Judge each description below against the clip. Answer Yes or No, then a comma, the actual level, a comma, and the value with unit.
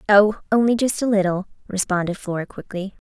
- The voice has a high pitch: Yes, high, 200 Hz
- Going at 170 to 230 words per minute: No, average, 155 wpm